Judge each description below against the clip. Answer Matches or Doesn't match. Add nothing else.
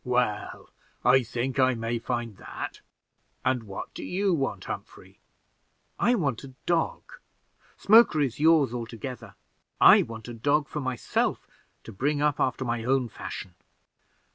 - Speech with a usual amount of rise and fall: Matches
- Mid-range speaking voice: Doesn't match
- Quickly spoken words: Doesn't match